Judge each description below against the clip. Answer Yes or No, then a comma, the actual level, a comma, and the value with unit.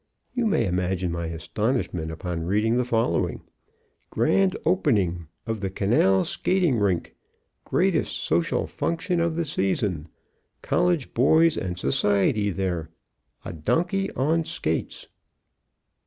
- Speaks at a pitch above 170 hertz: No, low, 105 Hz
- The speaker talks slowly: Yes, slow, 115 wpm